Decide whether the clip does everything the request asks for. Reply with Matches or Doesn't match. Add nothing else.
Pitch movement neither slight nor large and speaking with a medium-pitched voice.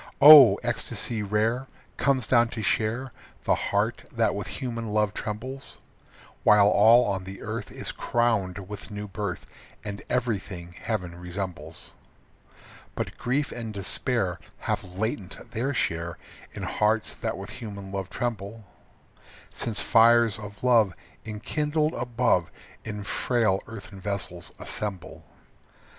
Doesn't match